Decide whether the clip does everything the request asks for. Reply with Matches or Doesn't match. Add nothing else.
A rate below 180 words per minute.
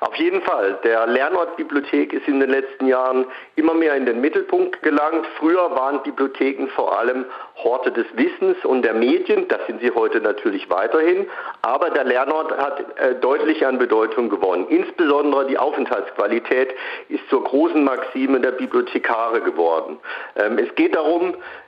Matches